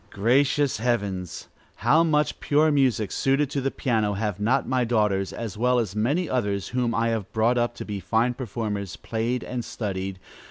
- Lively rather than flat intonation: No, average, 3.7 semitones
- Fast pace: No, average, 175 wpm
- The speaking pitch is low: Yes, low, 115 Hz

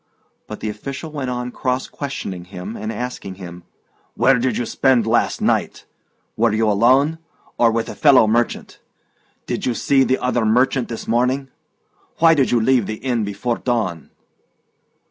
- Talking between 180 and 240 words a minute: No, average, 165 wpm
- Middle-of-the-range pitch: No, low, 120 Hz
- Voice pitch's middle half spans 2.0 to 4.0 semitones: Yes, average, 3.3 semitones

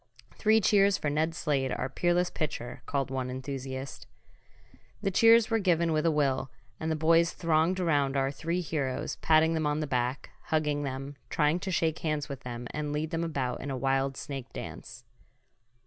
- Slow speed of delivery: No, average, 180 wpm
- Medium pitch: Yes, medium, 150 Hz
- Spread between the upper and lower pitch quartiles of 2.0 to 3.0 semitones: No, average, 3.5 semitones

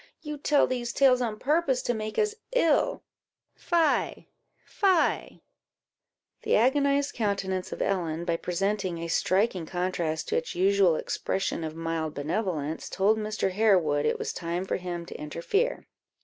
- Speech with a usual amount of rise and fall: No, wide, 7.1 semitones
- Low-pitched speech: No, high, 195 Hz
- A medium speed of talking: Yes, average, 145 wpm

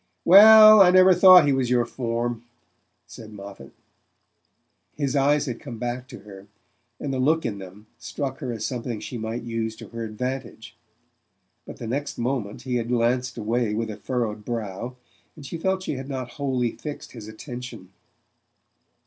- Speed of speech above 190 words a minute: No, average, 170 wpm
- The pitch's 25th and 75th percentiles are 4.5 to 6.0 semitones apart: No, average, 3.5 semitones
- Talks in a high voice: No, low, 120 Hz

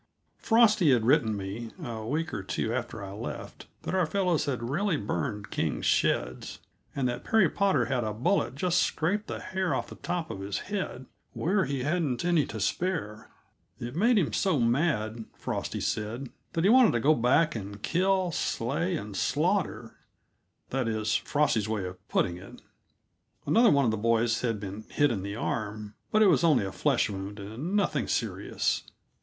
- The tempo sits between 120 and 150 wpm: No, average, 180 wpm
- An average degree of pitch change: No, wide, 8.1 semitones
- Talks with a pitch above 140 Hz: No, low, 125 Hz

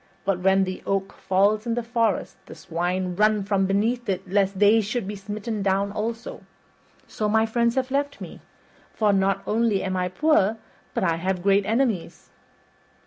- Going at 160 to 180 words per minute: Yes, average, 175 wpm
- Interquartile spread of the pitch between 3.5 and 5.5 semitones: No, average, 2.8 semitones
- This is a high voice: Yes, high, 200 Hz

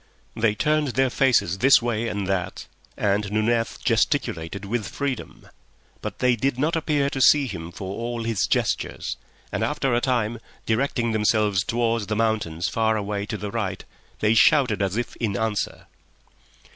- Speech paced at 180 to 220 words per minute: No, average, 160 wpm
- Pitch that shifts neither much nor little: Yes, average, 3.0 semitones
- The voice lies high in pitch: No, low, 110 Hz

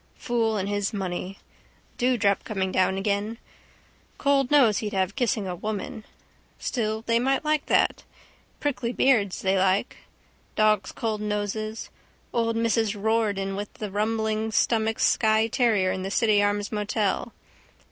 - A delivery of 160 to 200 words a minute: No, slow, 135 wpm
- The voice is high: Yes, high, 215 Hz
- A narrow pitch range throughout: Yes, narrow, 2.3 semitones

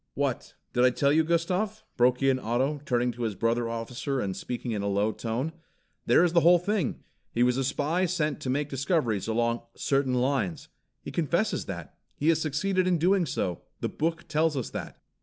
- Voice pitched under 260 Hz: Yes, low, 135 Hz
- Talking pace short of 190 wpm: No, average, 195 wpm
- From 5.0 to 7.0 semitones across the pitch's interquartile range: Yes, wide, 5.5 semitones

